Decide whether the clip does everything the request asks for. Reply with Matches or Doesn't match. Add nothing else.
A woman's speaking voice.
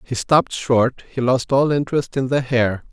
Doesn't match